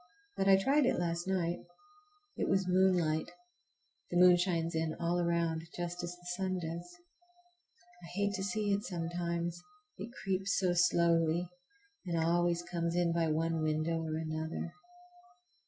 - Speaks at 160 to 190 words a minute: No, average, 150 wpm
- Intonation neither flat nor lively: No, narrow, 1.6 semitones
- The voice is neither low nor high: Yes, medium, 175 Hz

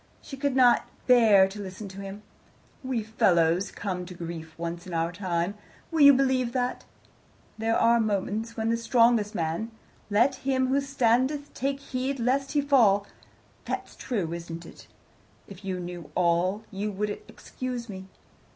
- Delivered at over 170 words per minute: No, average, 160 wpm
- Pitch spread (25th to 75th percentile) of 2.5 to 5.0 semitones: No, wide, 5.5 semitones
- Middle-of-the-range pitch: No, high, 215 Hz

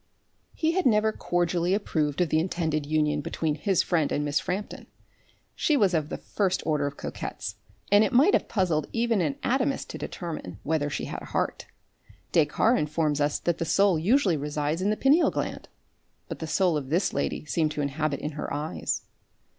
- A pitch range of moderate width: Yes, average, 5.0 semitones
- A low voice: No, medium, 165 Hz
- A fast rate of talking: No, average, 190 wpm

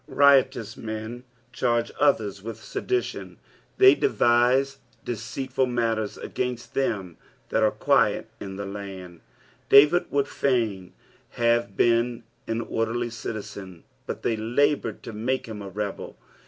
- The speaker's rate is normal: No, slow, 130 wpm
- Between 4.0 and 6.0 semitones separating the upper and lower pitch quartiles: No, average, 3.2 semitones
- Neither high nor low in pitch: No, low, 115 Hz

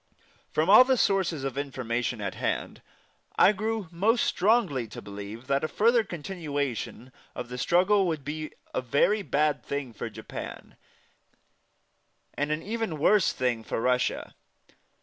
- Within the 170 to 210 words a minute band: No, average, 145 wpm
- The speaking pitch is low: No, medium, 150 Hz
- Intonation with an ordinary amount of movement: No, wide, 7.5 semitones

